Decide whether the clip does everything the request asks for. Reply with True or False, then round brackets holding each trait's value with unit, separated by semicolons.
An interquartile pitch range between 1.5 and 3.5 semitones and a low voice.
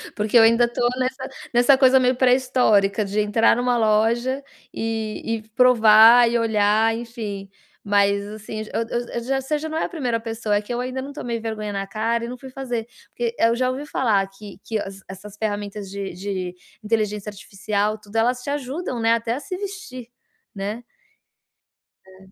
False (3.1 semitones; 225 Hz)